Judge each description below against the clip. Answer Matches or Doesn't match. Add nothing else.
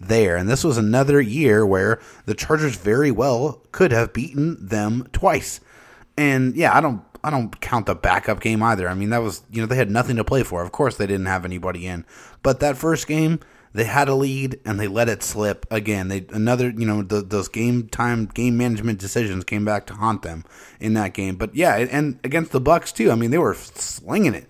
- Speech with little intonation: Doesn't match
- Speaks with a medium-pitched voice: Doesn't match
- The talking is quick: Matches